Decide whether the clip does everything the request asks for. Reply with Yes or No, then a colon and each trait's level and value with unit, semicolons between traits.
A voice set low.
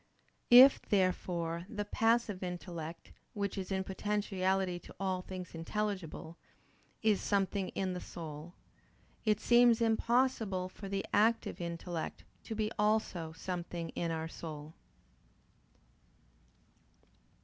No: high, 190 Hz